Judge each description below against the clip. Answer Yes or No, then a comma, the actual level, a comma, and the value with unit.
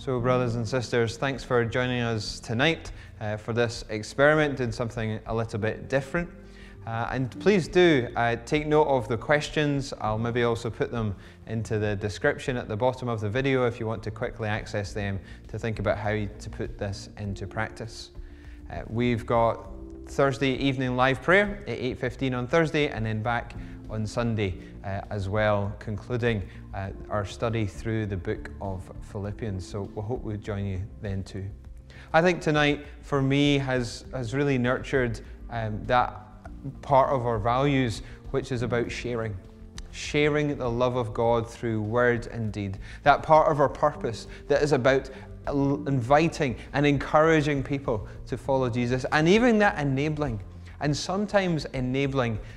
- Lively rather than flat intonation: No, average, 4.3 semitones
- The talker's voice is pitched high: No, low, 120 Hz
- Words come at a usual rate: Yes, average, 165 wpm